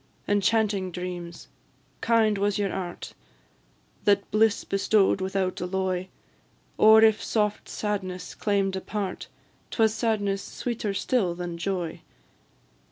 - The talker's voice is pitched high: Yes, high, 195 Hz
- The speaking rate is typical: No, slow, 110 wpm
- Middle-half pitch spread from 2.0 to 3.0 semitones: Yes, narrow, 2.6 semitones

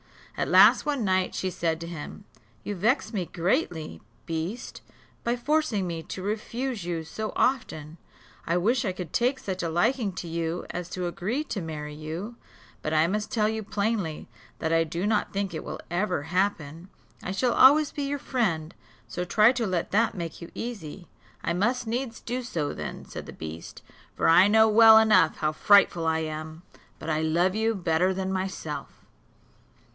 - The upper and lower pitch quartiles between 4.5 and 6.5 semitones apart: Yes, average, 5.2 semitones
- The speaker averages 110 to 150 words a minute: No, average, 180 wpm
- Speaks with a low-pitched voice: No, medium, 185 Hz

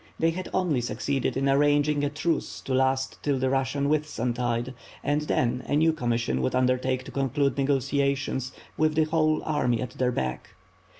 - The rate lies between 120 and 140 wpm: No, average, 175 wpm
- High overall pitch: No, low, 135 Hz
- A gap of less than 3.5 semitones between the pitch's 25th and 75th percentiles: Yes, average, 2.7 semitones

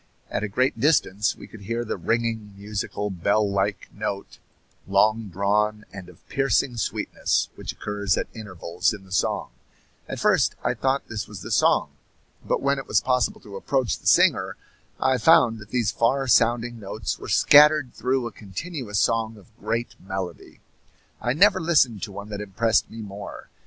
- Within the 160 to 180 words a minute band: Yes, average, 170 wpm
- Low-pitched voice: Yes, low, 110 Hz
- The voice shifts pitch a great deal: No, average, 3.5 semitones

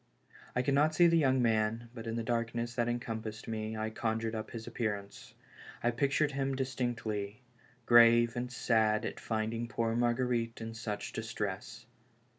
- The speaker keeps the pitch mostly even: Yes, narrow, 1.7 semitones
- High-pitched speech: No, low, 115 Hz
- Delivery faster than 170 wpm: No, average, 160 wpm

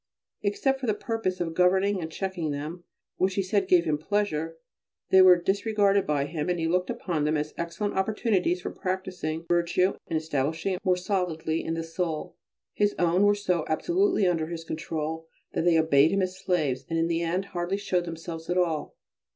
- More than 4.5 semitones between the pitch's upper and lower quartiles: No, average, 2.9 semitones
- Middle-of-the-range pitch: Yes, medium, 175 Hz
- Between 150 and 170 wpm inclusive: No, average, 190 wpm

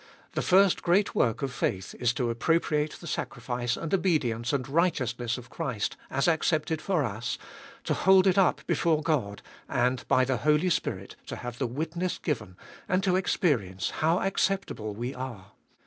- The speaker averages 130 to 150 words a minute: No, average, 170 wpm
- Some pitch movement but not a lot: No, wide, 6.1 semitones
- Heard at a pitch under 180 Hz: Yes, medium, 140 Hz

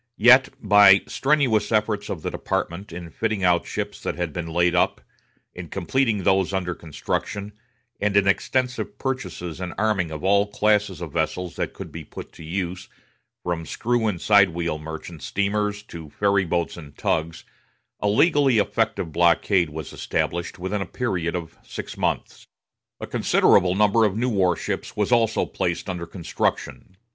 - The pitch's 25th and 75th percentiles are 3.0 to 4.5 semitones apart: Yes, average, 3.6 semitones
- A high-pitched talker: No, very low, 95 Hz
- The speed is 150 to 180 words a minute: Yes, average, 170 wpm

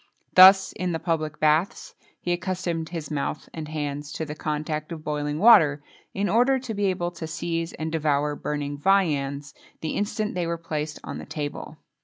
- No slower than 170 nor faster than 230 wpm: Yes, average, 180 wpm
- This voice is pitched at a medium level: Yes, medium, 160 Hz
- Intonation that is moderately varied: Yes, average, 3.1 semitones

